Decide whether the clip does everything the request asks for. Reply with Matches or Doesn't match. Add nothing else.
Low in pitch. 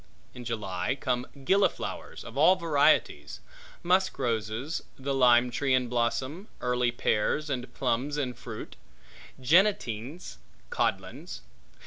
Matches